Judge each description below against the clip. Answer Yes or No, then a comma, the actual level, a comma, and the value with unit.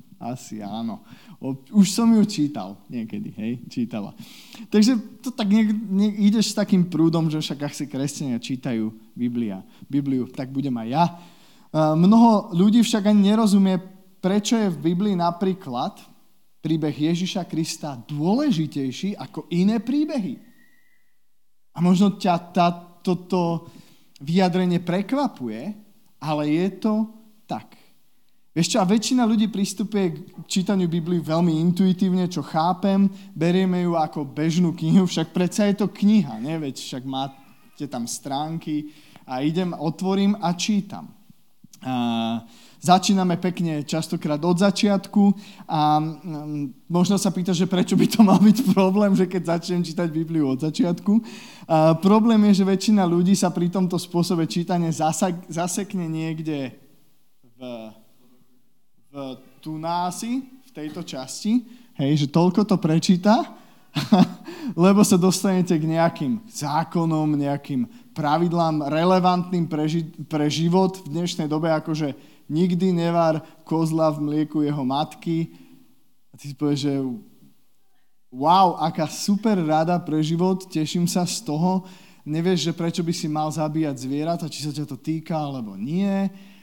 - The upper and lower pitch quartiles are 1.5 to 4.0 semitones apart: No, average, 4.5 semitones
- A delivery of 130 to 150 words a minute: Yes, average, 135 wpm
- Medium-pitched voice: Yes, medium, 175 Hz